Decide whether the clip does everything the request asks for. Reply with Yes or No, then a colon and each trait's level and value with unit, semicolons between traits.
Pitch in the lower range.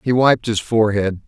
Yes: low, 110 Hz